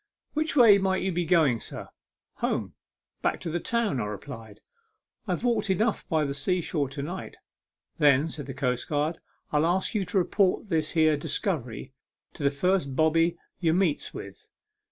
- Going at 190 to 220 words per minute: Yes, average, 195 wpm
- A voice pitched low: No, medium, 165 Hz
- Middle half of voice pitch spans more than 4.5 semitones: Yes, average, 5.0 semitones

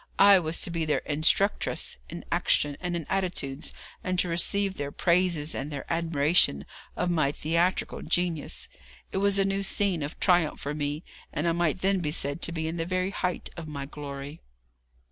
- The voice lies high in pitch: No, medium, 170 Hz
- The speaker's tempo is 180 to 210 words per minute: Yes, average, 185 wpm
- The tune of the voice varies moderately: Yes, average, 3.6 semitones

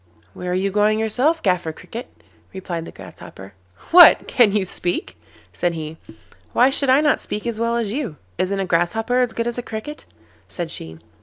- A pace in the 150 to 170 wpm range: No, average, 185 wpm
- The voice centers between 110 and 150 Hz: No, high, 210 Hz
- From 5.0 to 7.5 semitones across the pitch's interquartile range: Yes, wide, 5.4 semitones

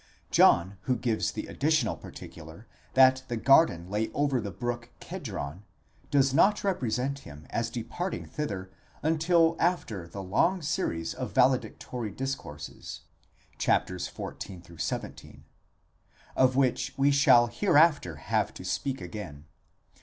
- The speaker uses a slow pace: Yes, slow, 125 wpm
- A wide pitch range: Yes, wide, 7.1 semitones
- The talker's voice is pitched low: Yes, low, 120 Hz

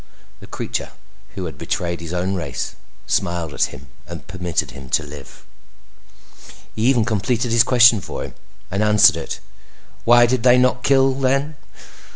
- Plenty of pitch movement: Yes, wide, 6.3 semitones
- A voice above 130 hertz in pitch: No, low, 105 Hz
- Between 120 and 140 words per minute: No, average, 160 wpm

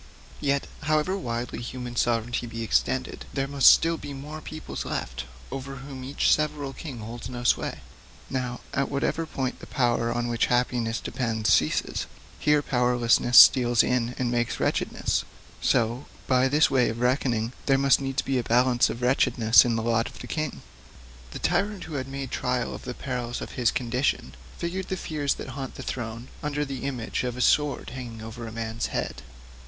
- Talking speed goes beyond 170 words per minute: Yes, average, 180 wpm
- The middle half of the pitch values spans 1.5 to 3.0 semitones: Yes, average, 2.7 semitones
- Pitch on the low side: Yes, low, 125 Hz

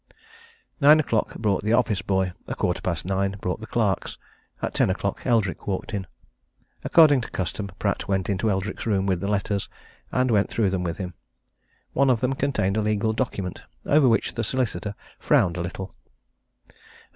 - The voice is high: No, low, 100 Hz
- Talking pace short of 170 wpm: No, average, 175 wpm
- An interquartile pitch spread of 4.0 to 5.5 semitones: No, average, 3.5 semitones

